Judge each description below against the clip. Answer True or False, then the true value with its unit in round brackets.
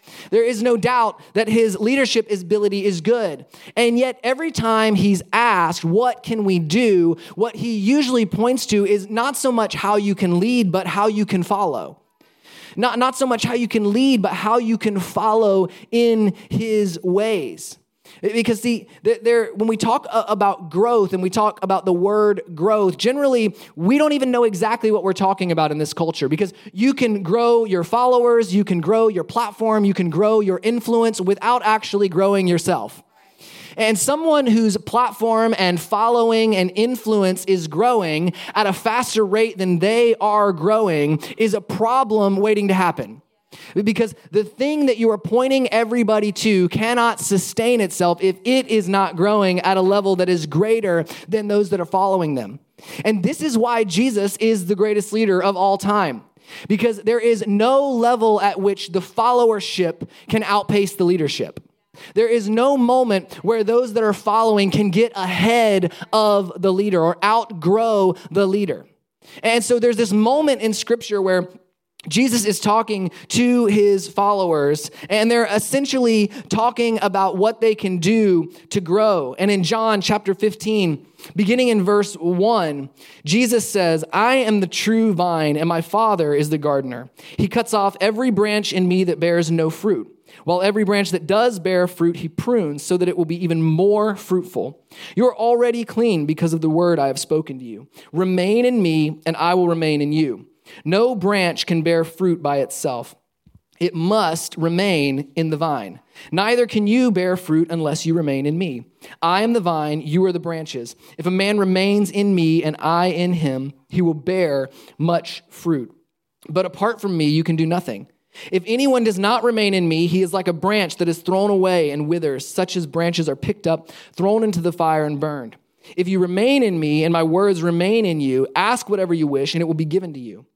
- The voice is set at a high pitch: True (200 Hz)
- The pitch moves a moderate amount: True (4.3 semitones)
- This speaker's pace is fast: False (185 wpm)